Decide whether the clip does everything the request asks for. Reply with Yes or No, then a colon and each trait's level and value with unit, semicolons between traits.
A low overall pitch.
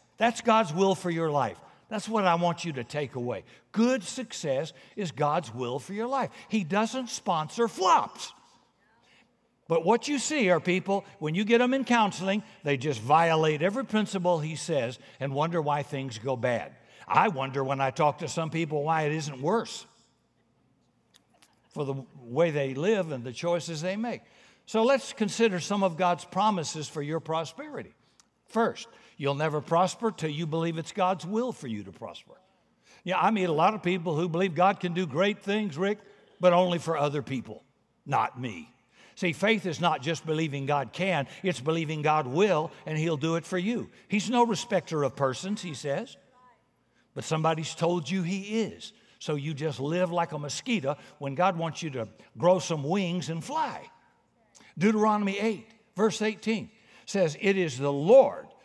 No: medium, 175 Hz